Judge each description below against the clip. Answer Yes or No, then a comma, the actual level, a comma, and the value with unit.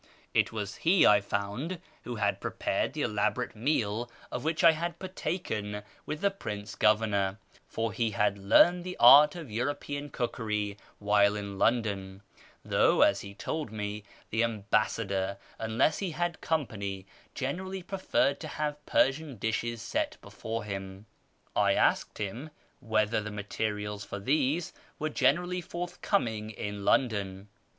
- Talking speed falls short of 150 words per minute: Yes, average, 140 wpm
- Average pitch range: No, wide, 6.6 semitones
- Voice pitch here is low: Yes, low, 110 Hz